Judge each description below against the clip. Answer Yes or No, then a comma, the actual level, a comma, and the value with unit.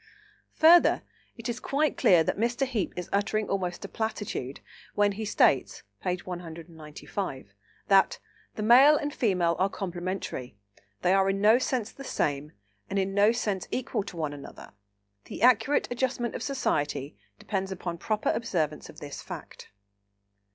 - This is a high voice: Yes, high, 195 Hz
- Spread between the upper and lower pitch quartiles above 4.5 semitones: Yes, average, 5.1 semitones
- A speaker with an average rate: Yes, average, 150 wpm